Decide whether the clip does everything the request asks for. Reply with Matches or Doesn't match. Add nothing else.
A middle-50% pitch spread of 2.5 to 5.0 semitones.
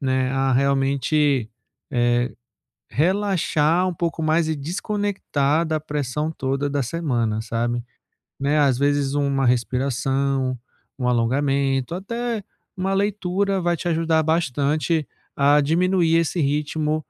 Matches